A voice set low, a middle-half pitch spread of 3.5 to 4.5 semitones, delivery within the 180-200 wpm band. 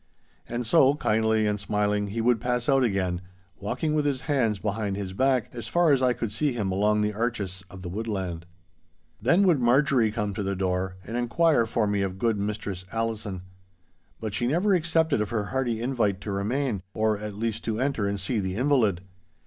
Yes: low, 110 Hz; average, 3.8 semitones; average, 195 wpm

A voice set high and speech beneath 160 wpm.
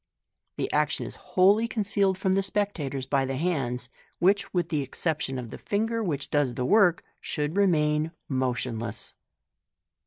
No: medium, 155 Hz; average, 150 wpm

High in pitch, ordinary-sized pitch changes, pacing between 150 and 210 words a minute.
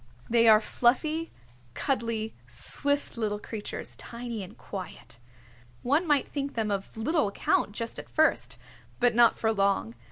No: high, 230 Hz; average, 4.8 semitones; average, 140 wpm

